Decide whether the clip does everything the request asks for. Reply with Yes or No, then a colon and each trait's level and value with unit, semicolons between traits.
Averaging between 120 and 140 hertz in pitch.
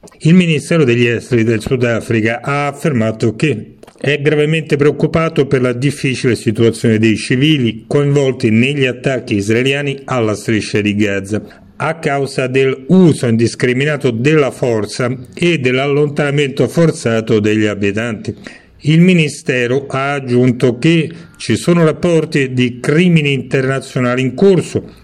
Yes: low, 135 Hz